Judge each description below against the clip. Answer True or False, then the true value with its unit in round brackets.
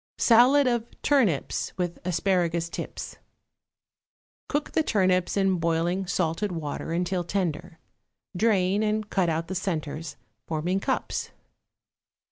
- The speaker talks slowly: True (110 wpm)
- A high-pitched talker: False (180 Hz)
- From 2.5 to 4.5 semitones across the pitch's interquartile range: True (3.6 semitones)